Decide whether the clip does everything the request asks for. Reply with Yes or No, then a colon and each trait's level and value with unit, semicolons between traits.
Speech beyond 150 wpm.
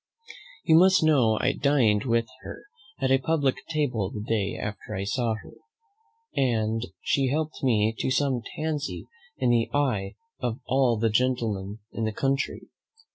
Yes: average, 160 wpm